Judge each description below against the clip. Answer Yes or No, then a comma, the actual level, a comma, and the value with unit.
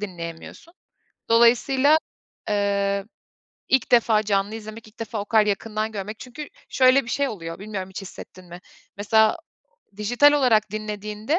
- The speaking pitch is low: No, high, 215 Hz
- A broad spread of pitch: No, average, 2.8 semitones